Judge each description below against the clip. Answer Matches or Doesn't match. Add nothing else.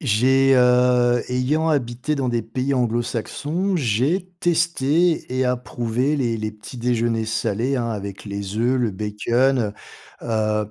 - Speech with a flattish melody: Doesn't match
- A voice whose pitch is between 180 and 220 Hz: Doesn't match